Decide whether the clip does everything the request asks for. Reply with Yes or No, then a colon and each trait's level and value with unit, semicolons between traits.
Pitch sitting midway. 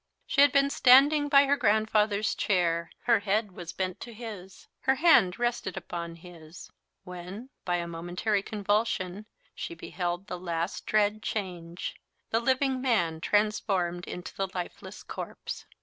No: high, 200 Hz